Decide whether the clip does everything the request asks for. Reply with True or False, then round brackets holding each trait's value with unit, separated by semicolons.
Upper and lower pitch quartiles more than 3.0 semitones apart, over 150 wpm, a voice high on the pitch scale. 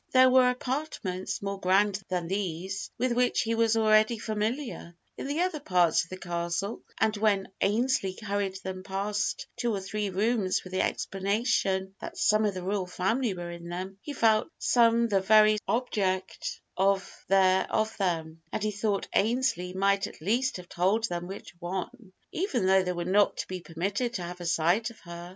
True (3.4 semitones; 185 wpm; 200 Hz)